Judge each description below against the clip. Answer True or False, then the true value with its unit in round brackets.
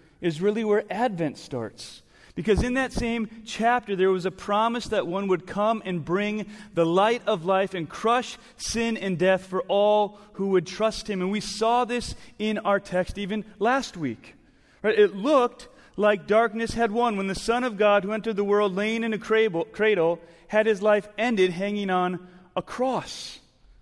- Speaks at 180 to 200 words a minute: True (185 wpm)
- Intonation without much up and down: False (3.2 semitones)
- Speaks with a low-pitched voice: False (210 Hz)